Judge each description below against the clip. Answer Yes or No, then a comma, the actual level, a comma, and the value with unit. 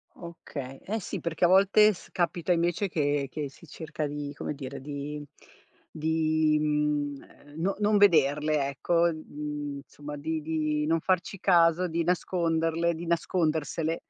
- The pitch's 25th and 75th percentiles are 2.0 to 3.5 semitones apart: Yes, narrow, 2.5 semitones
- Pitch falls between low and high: Yes, medium, 160 Hz